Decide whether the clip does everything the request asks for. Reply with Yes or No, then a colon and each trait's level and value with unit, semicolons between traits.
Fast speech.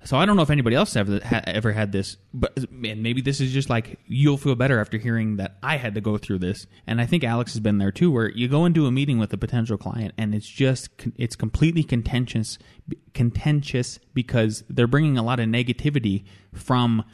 Yes: fast, 225 wpm